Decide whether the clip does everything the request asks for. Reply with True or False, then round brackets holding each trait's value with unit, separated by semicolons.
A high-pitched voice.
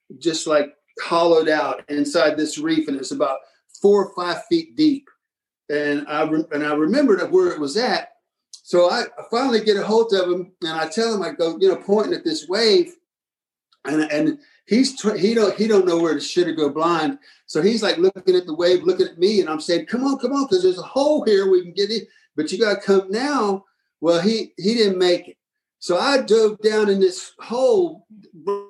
True (200 Hz)